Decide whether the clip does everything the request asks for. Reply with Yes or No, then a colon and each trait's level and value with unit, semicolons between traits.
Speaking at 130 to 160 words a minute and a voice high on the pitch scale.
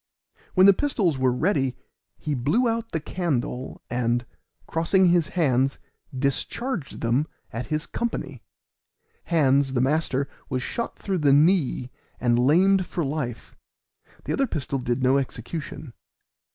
No: slow, 135 wpm; medium, 145 Hz